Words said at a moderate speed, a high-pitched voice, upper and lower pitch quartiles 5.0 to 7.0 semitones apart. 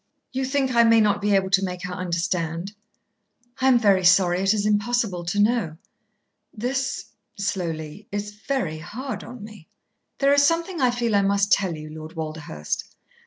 Yes: average, 175 wpm; high, 200 Hz; average, 5.3 semitones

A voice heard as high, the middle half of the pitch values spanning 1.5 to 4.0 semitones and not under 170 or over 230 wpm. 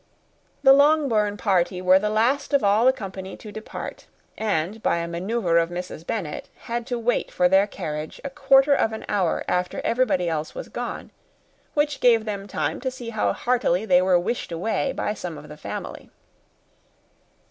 No: high, 210 Hz; average, 5.3 semitones; average, 180 wpm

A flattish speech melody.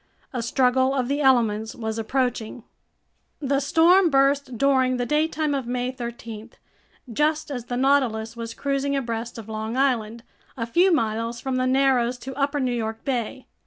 No: average, 3.1 semitones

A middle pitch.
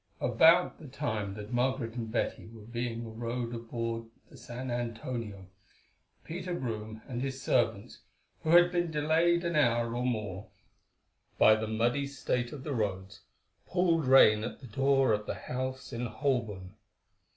No: low, 120 Hz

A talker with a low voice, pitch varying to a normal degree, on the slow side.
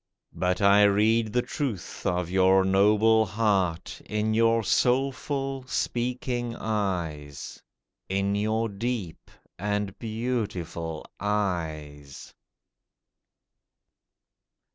Yes: low, 105 Hz; average, 3.7 semitones; slow, 80 wpm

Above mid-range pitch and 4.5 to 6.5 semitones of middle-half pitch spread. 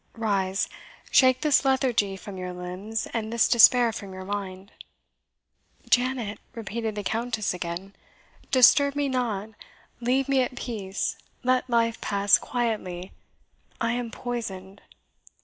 No: high, 225 Hz; average, 4.0 semitones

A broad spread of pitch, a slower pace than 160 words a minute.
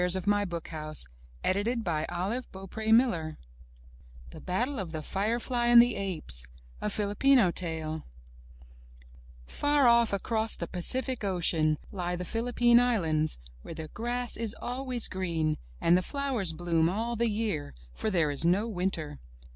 Yes: wide, 6.4 semitones; slow, 135 wpm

